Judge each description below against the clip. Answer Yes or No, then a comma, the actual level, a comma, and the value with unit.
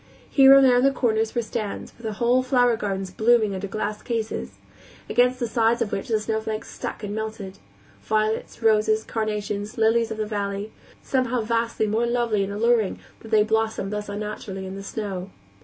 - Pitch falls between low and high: No, high, 220 Hz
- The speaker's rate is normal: Yes, average, 180 wpm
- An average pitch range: No, narrow, 2.0 semitones